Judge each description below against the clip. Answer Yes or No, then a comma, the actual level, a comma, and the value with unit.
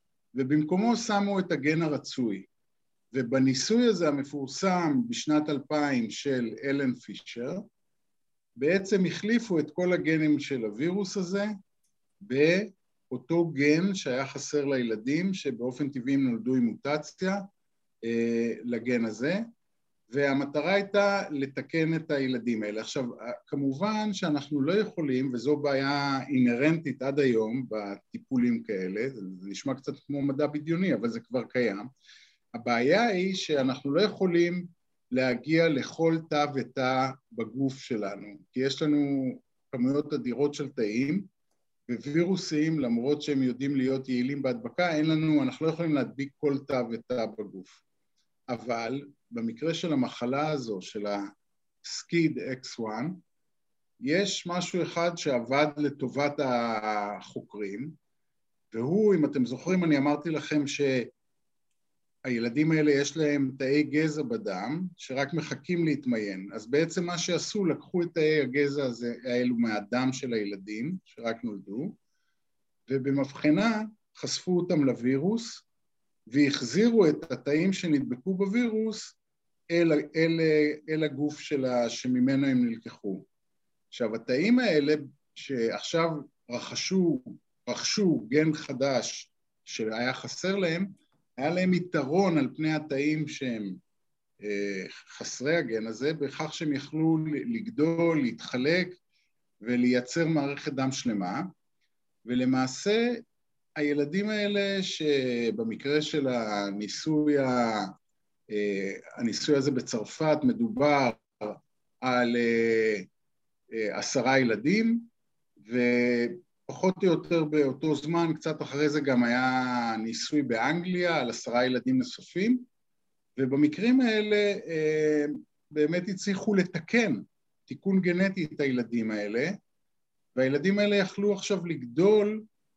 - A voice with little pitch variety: No, average, 5.3 semitones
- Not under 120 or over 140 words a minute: No, average, 105 wpm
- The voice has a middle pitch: Yes, medium, 145 Hz